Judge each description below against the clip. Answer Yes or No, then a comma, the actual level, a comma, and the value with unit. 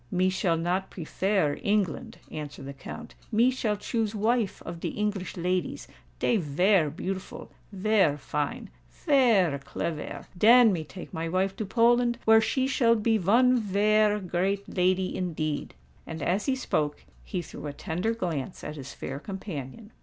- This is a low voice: No, high, 190 Hz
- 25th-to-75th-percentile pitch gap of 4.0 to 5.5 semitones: Yes, average, 4.8 semitones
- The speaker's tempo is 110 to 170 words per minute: Yes, average, 145 wpm